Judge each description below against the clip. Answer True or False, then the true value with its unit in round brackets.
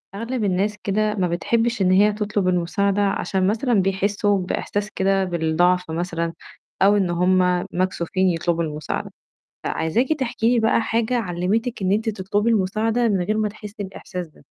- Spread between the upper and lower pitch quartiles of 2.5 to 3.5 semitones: True (2.9 semitones)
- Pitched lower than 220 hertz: True (195 Hz)